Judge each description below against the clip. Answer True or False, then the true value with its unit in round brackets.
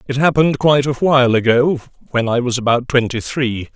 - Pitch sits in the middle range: False (130 Hz)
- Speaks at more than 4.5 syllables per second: True (6.0 syllables/s)